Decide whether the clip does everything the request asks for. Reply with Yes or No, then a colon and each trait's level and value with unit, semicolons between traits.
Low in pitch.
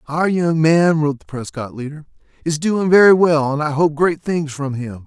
No: medium, 155 Hz